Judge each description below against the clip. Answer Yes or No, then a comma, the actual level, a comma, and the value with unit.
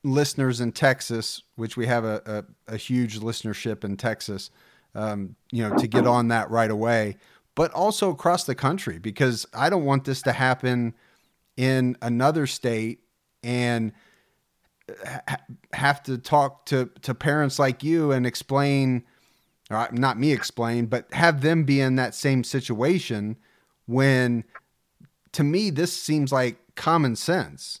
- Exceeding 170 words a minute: No, average, 150 wpm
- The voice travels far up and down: No, average, 3.3 semitones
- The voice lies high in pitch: No, low, 125 Hz